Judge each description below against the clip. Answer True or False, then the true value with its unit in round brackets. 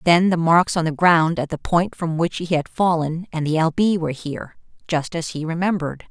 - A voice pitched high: False (165 Hz)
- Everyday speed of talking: False (235 wpm)